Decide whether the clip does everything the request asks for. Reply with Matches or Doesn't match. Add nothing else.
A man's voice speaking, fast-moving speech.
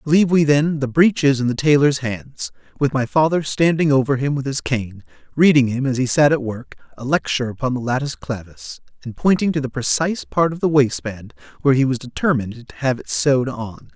Matches